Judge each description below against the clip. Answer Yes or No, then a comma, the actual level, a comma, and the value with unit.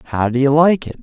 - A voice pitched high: No, medium, 140 Hz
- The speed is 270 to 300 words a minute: Yes, fast, 295 wpm